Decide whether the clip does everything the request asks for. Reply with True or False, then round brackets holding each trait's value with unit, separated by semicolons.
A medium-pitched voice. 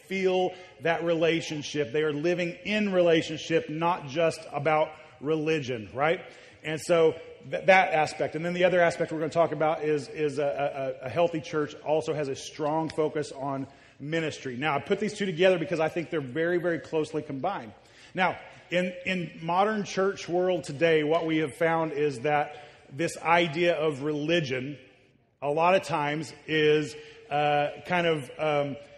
True (155 Hz)